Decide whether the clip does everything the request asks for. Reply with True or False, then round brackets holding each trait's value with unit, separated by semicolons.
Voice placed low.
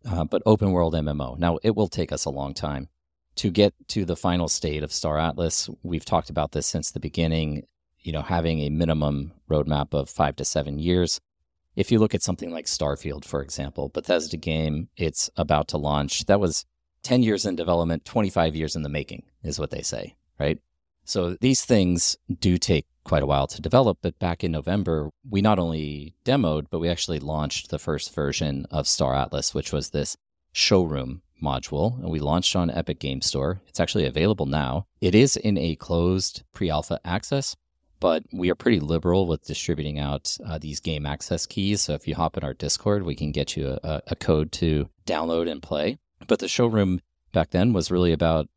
True (80 Hz)